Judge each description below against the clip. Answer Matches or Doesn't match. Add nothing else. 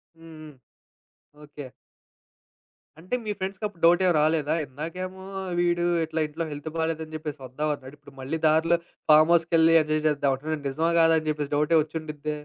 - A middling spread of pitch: Doesn't match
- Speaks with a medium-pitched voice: Matches